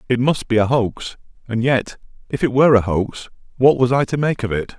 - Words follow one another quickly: Yes, fast, 240 wpm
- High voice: No, low, 120 Hz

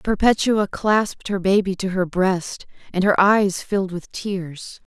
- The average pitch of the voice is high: Yes, high, 195 Hz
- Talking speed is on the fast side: No, average, 155 wpm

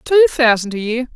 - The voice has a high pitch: Yes, high, 230 Hz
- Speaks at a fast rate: Yes, fast, 210 wpm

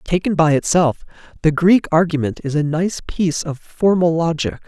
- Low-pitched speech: No, medium, 165 Hz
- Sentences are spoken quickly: No, average, 165 wpm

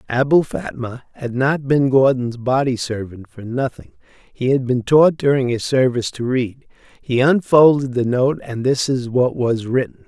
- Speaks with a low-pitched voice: Yes, low, 130 Hz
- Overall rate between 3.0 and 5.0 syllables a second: Yes, 4.5 syllables/s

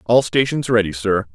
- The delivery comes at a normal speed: Yes, average, 180 wpm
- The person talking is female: No, male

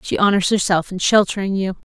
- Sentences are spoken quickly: No, average, 190 wpm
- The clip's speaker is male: No, female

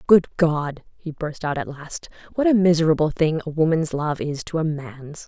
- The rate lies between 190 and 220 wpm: Yes, fast, 205 wpm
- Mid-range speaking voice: Yes, medium, 160 Hz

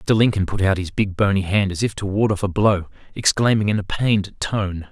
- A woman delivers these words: No, male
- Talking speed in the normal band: No, fast, 245 wpm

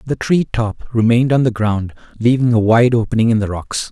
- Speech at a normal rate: No, fast, 215 wpm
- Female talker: No, male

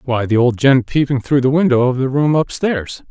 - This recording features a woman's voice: No, male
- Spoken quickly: Yes, fast, 230 wpm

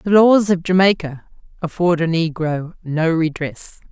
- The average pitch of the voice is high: No, medium, 170 Hz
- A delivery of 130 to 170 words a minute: Yes, average, 140 wpm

